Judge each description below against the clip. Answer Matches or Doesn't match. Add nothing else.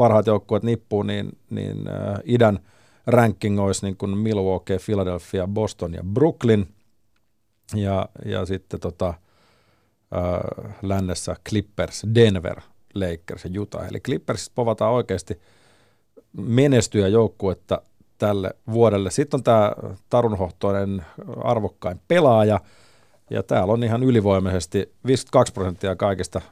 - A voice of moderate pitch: Doesn't match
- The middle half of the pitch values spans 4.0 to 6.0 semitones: Doesn't match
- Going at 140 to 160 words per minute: Doesn't match